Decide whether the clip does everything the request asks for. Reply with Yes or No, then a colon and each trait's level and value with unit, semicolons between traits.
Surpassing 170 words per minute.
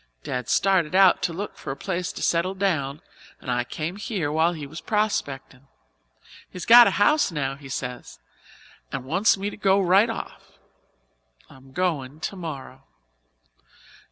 No: average, 155 wpm